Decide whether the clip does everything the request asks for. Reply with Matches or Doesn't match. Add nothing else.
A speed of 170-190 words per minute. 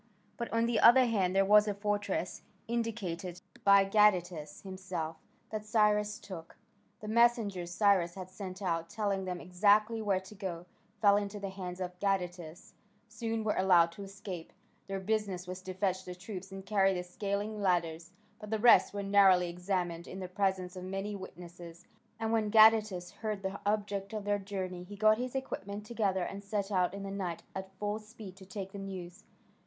Matches